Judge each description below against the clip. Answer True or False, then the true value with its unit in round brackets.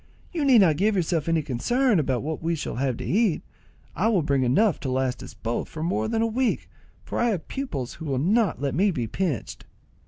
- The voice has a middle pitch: True (165 Hz)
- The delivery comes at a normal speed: False (225 wpm)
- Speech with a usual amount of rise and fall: False (8.2 semitones)